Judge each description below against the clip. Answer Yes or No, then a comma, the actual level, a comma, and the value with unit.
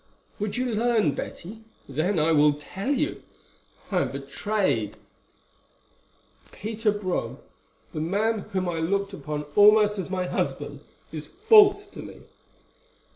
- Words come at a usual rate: No, slow, 130 wpm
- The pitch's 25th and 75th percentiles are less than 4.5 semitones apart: No, average, 5.1 semitones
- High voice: Yes, high, 200 Hz